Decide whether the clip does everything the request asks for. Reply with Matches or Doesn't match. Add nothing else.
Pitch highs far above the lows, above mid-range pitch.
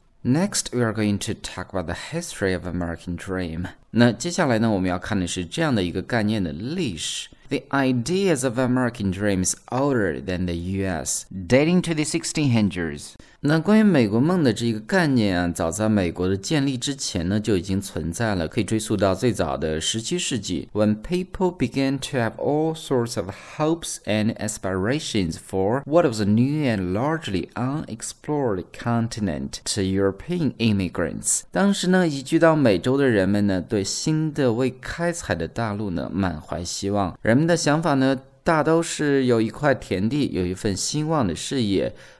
Doesn't match